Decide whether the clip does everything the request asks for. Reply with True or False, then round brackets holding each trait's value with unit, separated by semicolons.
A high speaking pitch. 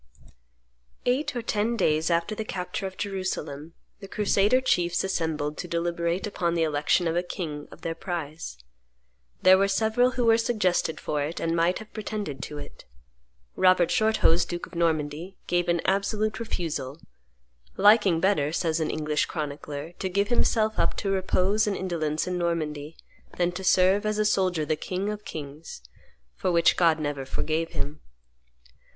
False (175 Hz)